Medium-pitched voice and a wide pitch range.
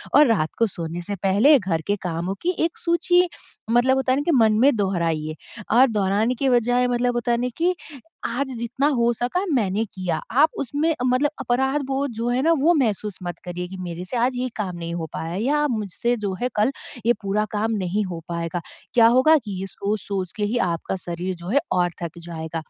No: high, 225 Hz; wide, 6.0 semitones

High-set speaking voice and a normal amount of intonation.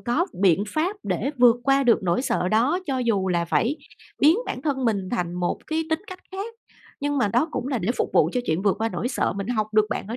No: high, 245 Hz; wide, 6.4 semitones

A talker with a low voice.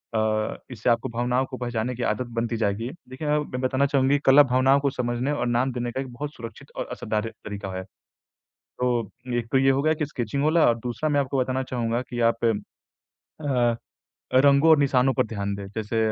Yes: low, 125 Hz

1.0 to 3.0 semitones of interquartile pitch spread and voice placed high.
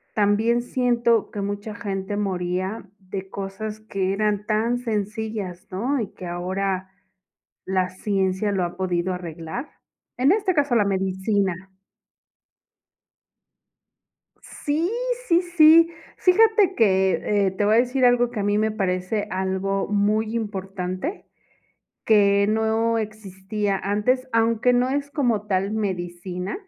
No: average, 3.5 semitones; high, 205 Hz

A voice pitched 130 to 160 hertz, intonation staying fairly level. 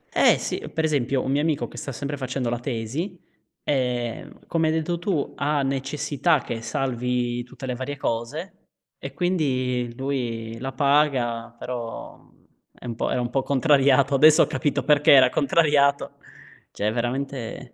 No: low, 135 Hz; average, 3.2 semitones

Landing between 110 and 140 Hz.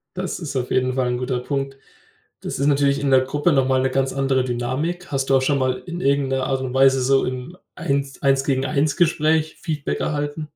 Yes: low, 135 Hz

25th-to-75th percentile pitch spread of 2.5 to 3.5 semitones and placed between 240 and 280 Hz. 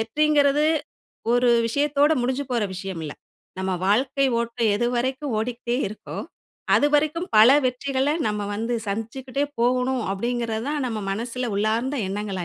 No: average, 3.9 semitones; high, 245 Hz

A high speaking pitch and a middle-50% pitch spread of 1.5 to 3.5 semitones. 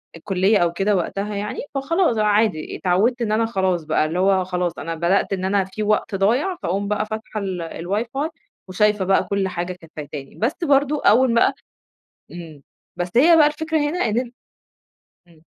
No: high, 200 Hz; average, 4.5 semitones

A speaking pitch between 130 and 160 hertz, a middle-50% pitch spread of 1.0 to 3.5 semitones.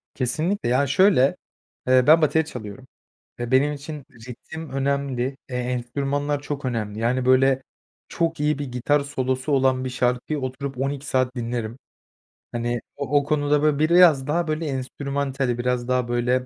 Yes: low, 135 Hz; narrow, 2.5 semitones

